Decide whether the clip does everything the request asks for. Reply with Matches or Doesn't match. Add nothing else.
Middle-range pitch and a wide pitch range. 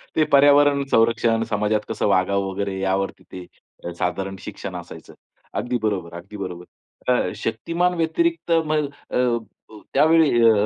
Doesn't match